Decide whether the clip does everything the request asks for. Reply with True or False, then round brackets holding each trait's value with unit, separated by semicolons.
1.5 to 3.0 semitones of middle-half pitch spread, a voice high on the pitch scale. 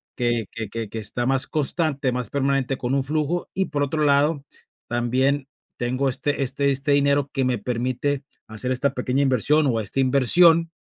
False (2.5 semitones; 135 Hz)